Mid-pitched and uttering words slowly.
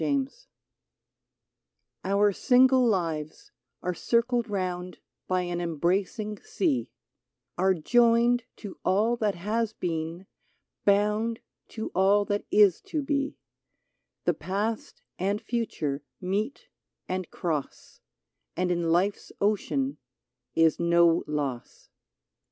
No: high, 200 Hz; slow, 105 wpm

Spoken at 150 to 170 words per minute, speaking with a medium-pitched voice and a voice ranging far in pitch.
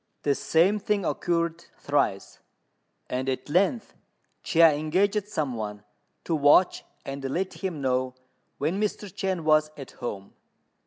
No: slow, 135 wpm; medium, 155 Hz; wide, 5.8 semitones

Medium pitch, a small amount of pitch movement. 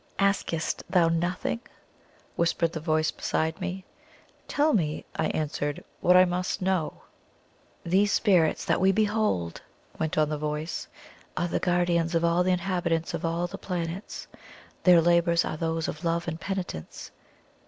Yes: medium, 170 Hz; narrow, 2.1 semitones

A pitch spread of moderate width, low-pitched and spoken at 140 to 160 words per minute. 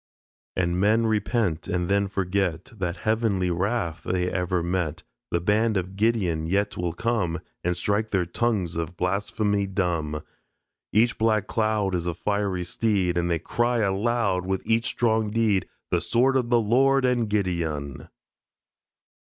Yes: average, 4.0 semitones; low, 100 Hz; average, 150 wpm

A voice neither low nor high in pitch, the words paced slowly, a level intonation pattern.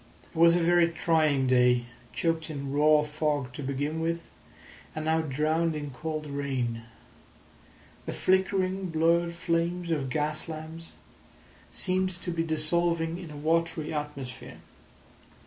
Yes: medium, 160 Hz; slow, 130 wpm; narrow, 2.3 semitones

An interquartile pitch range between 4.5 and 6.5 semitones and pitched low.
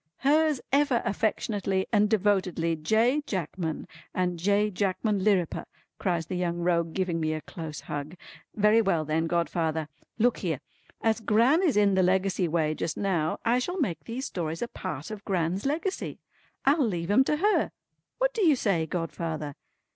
No: average, 5.3 semitones; high, 190 Hz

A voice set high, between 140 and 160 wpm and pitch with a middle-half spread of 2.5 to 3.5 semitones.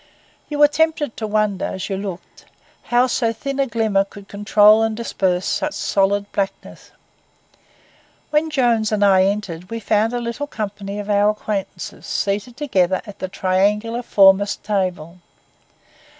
Yes: high, 210 Hz; average, 150 wpm; average, 3.0 semitones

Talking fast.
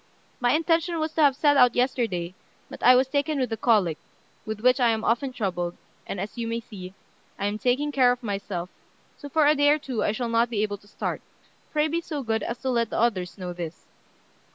Yes: fast, 230 wpm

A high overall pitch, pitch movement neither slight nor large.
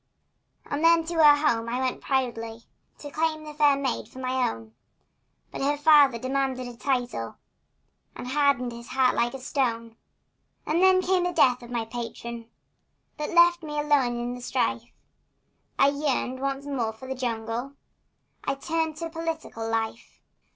Yes: very high, 265 Hz; average, 3.9 semitones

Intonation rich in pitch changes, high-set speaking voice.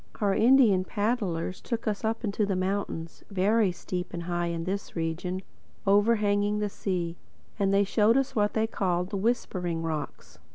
No: average, 3.0 semitones; high, 195 Hz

